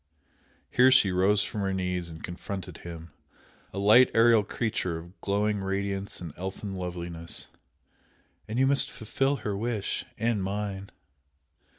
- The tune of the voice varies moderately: Yes, average, 3.0 semitones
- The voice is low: Yes, low, 100 Hz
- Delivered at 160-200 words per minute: No, slow, 135 wpm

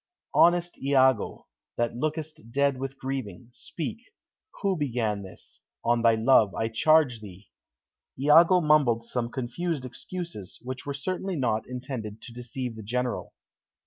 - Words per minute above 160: No, slow, 135 wpm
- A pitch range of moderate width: Yes, average, 4.6 semitones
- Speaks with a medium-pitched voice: No, low, 130 Hz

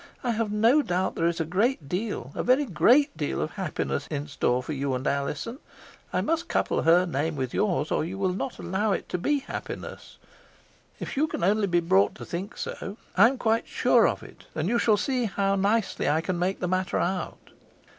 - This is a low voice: No, high, 190 Hz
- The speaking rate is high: Yes, fast, 215 wpm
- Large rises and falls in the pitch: Yes, wide, 5.9 semitones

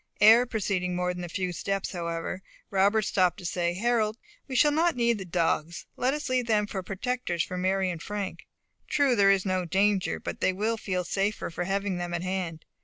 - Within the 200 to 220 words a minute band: Yes, fast, 205 wpm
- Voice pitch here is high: Yes, high, 195 Hz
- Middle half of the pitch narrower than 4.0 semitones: Yes, average, 3.4 semitones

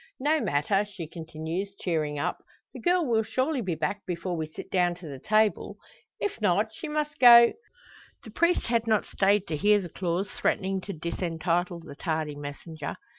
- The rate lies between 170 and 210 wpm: Yes, average, 180 wpm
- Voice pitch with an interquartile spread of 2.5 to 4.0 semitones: No, average, 5.2 semitones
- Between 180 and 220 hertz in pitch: Yes, high, 190 Hz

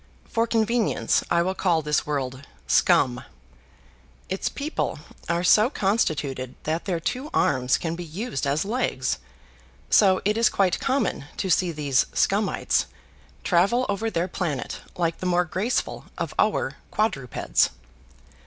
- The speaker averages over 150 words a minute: No, slow, 135 wpm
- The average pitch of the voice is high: No, medium, 175 Hz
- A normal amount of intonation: No, wide, 6.1 semitones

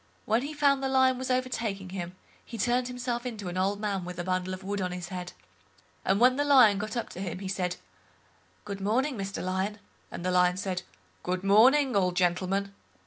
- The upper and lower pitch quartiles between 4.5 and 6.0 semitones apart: Yes, average, 5.1 semitones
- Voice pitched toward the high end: Yes, high, 195 Hz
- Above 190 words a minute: Yes, average, 200 wpm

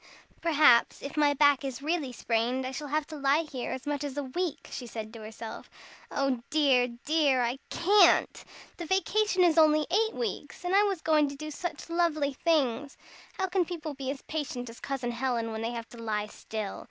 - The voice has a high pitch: Yes, very high, 285 Hz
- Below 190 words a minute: No, average, 200 wpm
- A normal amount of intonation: Yes, average, 4.6 semitones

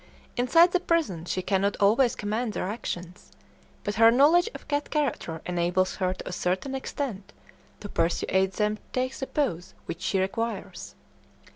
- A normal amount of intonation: No, wide, 6.1 semitones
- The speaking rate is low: No, average, 160 wpm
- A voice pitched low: No, high, 210 Hz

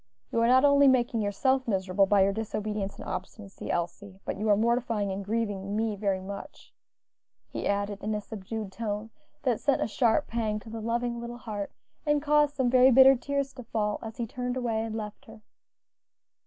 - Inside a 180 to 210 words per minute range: Yes, average, 190 wpm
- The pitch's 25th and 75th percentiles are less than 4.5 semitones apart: Yes, average, 3.2 semitones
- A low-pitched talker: No, high, 225 Hz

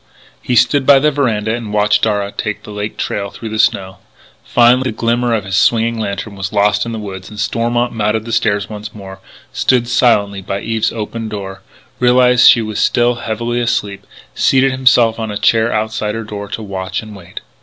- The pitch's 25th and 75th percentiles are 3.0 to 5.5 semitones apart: No, narrow, 2.5 semitones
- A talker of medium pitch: No, low, 110 Hz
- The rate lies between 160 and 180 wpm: No, average, 200 wpm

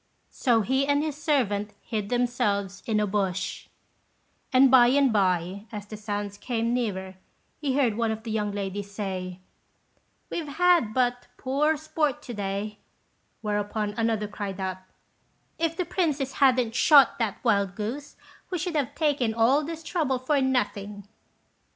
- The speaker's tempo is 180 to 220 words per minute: No, average, 150 wpm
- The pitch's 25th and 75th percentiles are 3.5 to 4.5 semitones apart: No, average, 5.2 semitones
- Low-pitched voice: No, high, 230 Hz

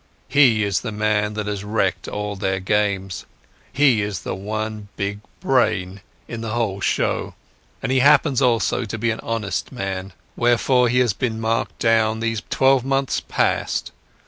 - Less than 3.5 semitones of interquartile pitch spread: Yes, average, 2.9 semitones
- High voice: No, low, 110 Hz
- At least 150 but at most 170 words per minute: Yes, average, 165 wpm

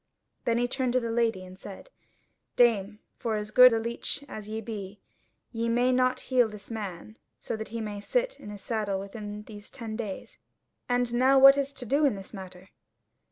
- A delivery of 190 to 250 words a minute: Yes, average, 200 wpm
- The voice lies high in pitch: Yes, high, 225 Hz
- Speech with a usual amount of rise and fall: Yes, average, 3.0 semitones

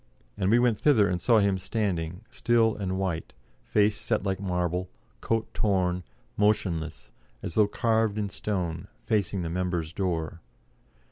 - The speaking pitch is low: Yes, very low, 95 Hz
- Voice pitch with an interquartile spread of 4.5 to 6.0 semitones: No, average, 3.2 semitones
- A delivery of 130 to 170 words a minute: Yes, average, 145 wpm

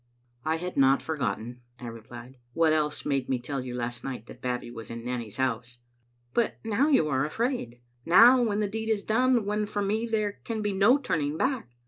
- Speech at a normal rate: No, fast, 210 wpm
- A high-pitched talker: No, medium, 150 Hz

